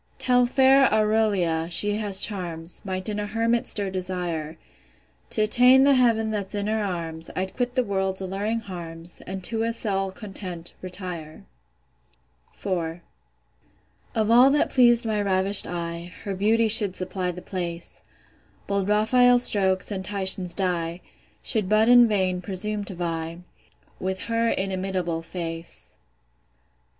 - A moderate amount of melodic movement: Yes, average, 3.5 semitones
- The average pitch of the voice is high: Yes, high, 195 Hz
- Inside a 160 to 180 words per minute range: No, average, 140 wpm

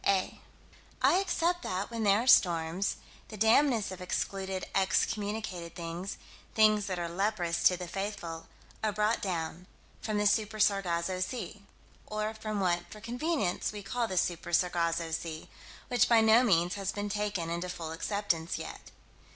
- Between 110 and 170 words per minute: Yes, average, 160 wpm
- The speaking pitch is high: Yes, high, 195 Hz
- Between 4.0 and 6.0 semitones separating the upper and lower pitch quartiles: No, average, 3.6 semitones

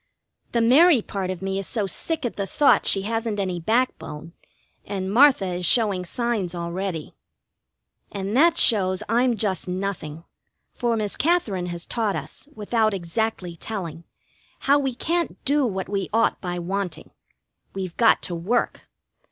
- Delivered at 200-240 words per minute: No, average, 150 wpm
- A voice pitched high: Yes, high, 200 Hz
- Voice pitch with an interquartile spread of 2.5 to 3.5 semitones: No, average, 4.4 semitones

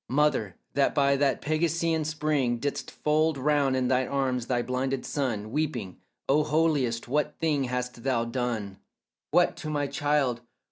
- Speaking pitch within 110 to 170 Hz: Yes, low, 135 Hz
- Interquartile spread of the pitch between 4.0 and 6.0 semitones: No, average, 3.4 semitones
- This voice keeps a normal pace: Yes, average, 150 wpm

